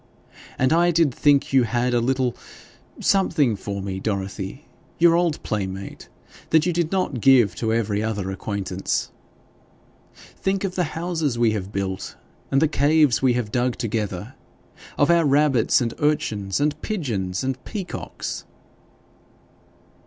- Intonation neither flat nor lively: No, wide, 6.9 semitones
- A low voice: Yes, low, 125 Hz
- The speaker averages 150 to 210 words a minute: No, average, 140 wpm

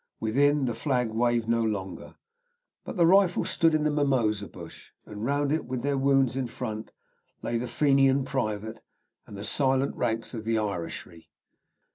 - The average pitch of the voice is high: No, low, 125 Hz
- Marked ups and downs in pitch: No, average, 4.0 semitones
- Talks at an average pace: Yes, average, 165 wpm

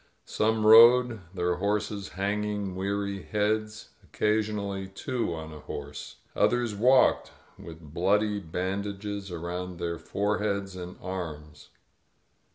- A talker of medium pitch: No, low, 100 Hz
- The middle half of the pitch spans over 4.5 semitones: No, average, 3.0 semitones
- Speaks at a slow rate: Yes, slow, 110 wpm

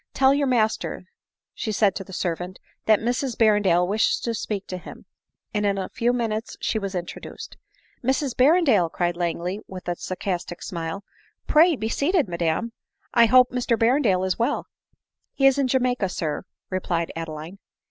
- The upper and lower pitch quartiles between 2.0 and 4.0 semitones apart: No, wide, 5.5 semitones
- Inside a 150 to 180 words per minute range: No, average, 190 wpm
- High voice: Yes, high, 210 Hz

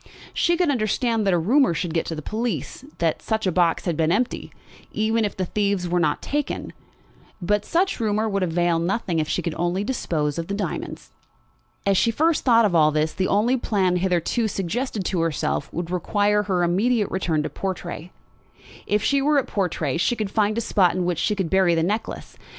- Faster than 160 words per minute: Yes, average, 200 wpm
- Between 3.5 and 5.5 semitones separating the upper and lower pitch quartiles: Yes, average, 4.3 semitones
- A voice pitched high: Yes, high, 195 Hz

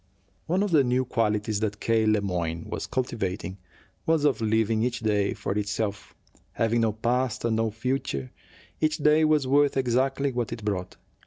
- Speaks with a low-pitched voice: Yes, low, 115 Hz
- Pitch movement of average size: Yes, average, 4.0 semitones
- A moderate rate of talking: Yes, average, 170 wpm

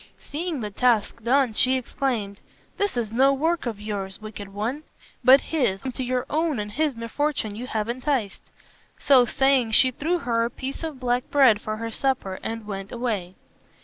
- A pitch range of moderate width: Yes, average, 4.0 semitones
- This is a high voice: Yes, high, 245 Hz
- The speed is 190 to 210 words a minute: No, average, 180 wpm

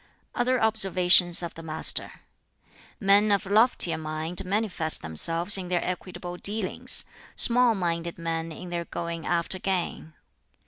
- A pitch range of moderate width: Yes, average, 3.2 semitones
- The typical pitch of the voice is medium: Yes, medium, 180 Hz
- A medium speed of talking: No, slow, 130 wpm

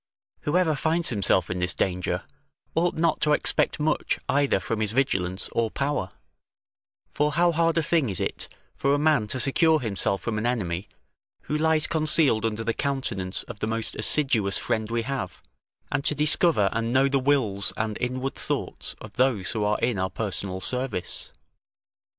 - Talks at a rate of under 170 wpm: No, average, 175 wpm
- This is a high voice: No, low, 120 Hz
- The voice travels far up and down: Yes, wide, 6.3 semitones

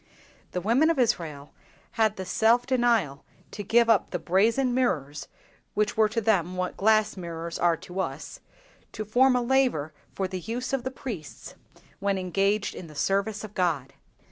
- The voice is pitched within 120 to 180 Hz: No, high, 205 Hz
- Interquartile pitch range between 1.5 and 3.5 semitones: No, average, 4.9 semitones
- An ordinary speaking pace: Yes, average, 165 wpm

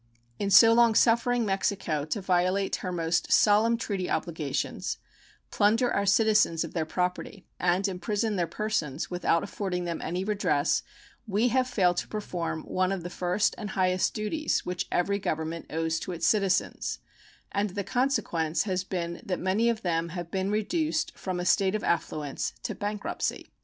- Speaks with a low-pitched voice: No, high, 190 Hz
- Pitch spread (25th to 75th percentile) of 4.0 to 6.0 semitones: No, average, 3.4 semitones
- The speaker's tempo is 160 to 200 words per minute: Yes, average, 165 wpm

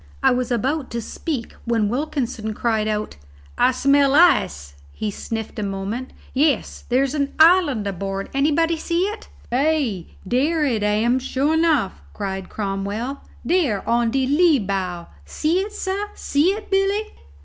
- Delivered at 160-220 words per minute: No, average, 150 wpm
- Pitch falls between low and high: No, very high, 255 Hz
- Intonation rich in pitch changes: Yes, wide, 6.8 semitones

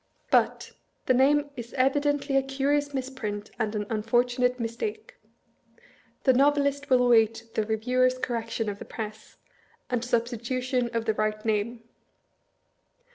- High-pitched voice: Yes, high, 245 Hz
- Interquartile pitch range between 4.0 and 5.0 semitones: No, average, 3.1 semitones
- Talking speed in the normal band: No, slow, 130 wpm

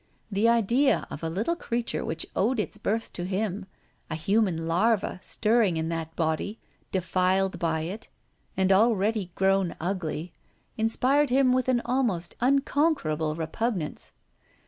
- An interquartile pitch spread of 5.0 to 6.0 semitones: Yes, wide, 5.6 semitones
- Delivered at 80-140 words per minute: Yes, slow, 135 wpm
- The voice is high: Yes, high, 195 Hz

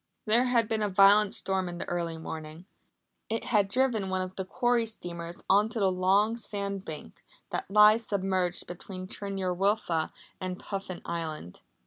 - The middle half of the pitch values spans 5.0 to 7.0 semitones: No, average, 3.1 semitones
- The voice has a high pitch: Yes, high, 195 Hz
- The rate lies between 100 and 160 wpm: No, average, 170 wpm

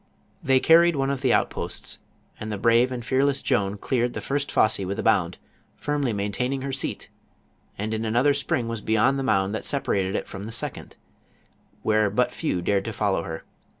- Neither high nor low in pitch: No, low, 115 Hz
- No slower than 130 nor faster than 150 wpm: No, average, 190 wpm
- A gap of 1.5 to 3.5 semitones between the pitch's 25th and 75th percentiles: No, average, 4.7 semitones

